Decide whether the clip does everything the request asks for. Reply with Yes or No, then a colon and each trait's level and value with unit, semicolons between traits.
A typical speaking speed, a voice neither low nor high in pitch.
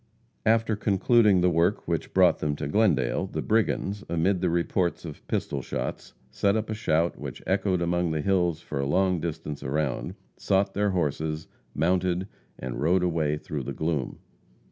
No: average, 165 wpm; very low, 85 Hz